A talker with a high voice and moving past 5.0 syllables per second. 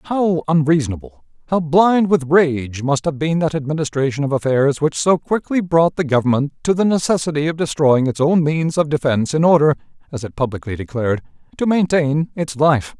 No: medium, 150 Hz; 5.3 syllables/s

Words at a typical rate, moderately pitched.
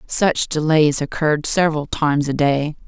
Yes: average, 145 wpm; medium, 150 Hz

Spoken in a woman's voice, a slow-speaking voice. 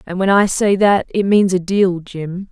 No: female; fast, 240 wpm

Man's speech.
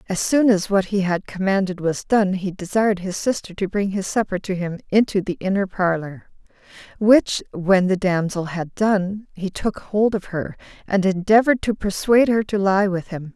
No: female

